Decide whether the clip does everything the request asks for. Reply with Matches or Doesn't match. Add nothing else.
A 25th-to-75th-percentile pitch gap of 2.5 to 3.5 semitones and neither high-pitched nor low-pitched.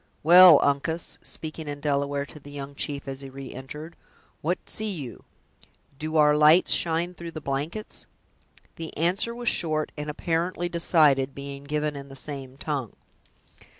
Matches